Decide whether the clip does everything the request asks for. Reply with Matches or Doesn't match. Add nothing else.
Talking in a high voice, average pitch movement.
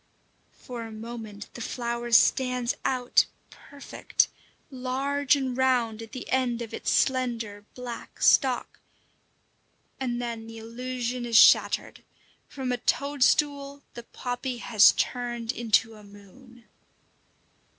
Doesn't match